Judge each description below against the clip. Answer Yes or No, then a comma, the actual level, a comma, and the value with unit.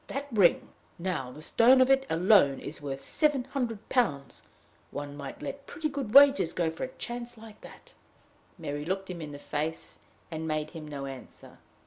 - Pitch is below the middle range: No, medium, 180 Hz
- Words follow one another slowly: No, average, 180 wpm